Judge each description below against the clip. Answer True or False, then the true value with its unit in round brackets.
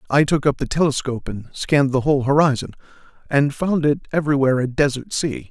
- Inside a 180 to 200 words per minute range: True (185 wpm)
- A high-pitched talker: False (140 Hz)